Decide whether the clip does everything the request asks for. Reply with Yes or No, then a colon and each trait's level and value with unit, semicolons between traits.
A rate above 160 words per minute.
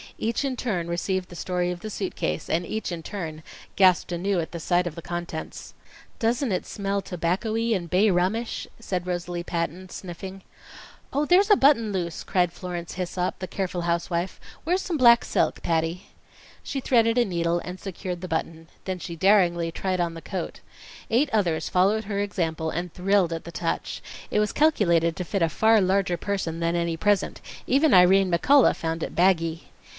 Yes: average, 180 wpm